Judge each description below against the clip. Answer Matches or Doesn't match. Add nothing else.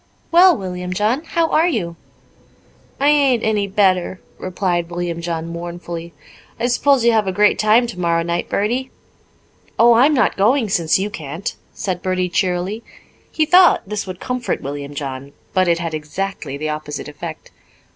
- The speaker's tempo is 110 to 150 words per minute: Doesn't match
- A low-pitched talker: Doesn't match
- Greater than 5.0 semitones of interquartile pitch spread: Matches